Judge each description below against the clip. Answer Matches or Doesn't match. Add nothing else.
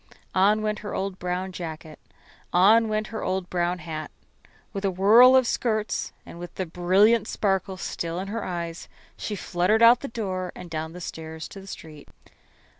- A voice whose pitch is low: Doesn't match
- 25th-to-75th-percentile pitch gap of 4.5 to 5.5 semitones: Doesn't match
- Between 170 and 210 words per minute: Matches